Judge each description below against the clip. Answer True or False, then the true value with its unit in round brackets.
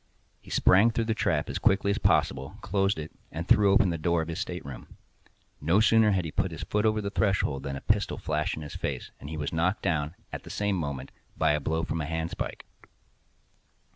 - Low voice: True (85 Hz)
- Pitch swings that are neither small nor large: True (4.8 semitones)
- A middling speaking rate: False (220 wpm)